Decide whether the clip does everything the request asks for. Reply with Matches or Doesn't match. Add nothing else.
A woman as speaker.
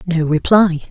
Matches